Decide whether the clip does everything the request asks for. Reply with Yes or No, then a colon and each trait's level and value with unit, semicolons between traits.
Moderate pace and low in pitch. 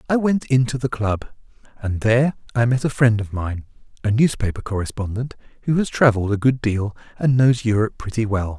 Yes: average, 175 wpm; low, 115 Hz